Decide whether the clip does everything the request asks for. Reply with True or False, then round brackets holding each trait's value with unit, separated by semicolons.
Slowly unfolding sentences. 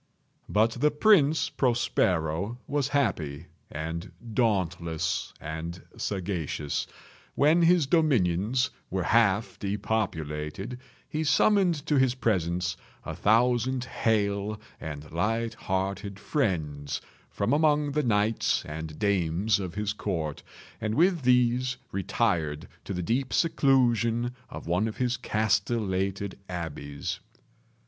True (110 wpm)